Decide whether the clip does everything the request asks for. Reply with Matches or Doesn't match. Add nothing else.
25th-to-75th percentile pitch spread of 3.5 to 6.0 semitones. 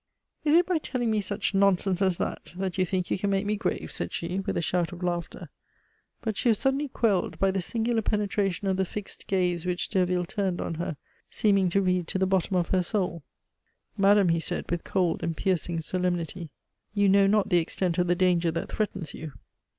Doesn't match